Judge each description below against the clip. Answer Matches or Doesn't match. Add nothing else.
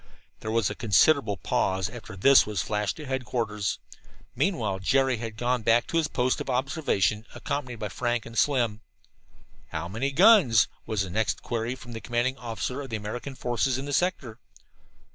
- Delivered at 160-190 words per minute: Matches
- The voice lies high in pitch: Doesn't match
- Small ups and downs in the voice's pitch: Doesn't match